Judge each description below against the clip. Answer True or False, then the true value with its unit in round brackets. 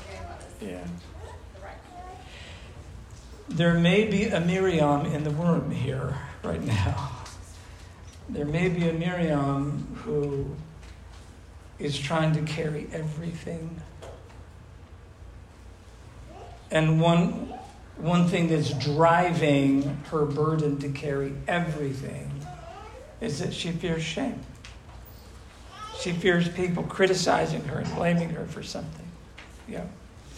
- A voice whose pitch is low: False (145 Hz)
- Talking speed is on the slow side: True (100 wpm)